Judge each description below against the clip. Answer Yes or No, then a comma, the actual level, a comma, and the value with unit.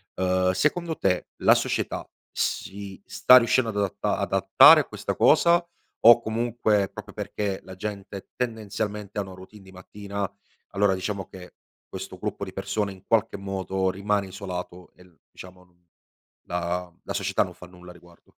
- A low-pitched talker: Yes, low, 100 Hz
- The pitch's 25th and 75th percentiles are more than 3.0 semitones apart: No, narrow, 2.4 semitones